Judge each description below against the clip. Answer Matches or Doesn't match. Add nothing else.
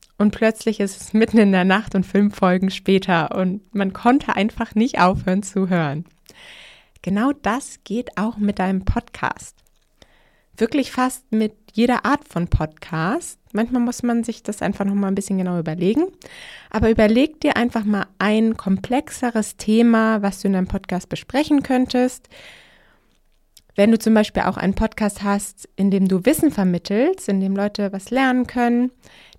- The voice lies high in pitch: Matches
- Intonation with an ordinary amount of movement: Matches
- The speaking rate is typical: Matches